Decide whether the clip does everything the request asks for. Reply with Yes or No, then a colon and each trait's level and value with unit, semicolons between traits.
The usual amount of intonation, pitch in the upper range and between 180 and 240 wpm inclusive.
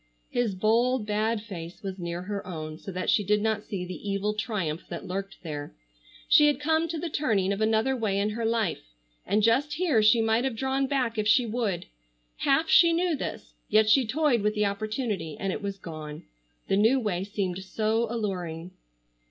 Yes: average, 3.9 semitones; high, 215 Hz; average, 195 wpm